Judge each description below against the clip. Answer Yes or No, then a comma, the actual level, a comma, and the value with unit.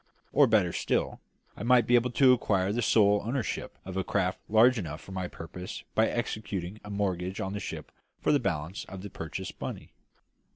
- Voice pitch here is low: Yes, low, 100 Hz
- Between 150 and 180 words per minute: No, average, 195 wpm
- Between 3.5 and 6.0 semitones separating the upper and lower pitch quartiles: Yes, average, 3.9 semitones